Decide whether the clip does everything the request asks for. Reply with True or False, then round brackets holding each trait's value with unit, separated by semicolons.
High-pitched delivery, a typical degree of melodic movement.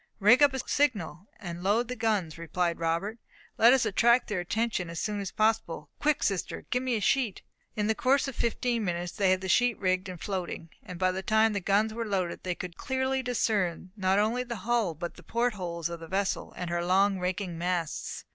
True (200 Hz; 4.5 semitones)